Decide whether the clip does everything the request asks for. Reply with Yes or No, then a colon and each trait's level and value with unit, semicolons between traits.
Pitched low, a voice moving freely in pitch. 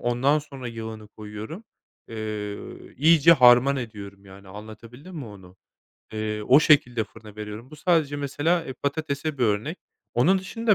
Yes: low, 120 Hz; wide, 5.9 semitones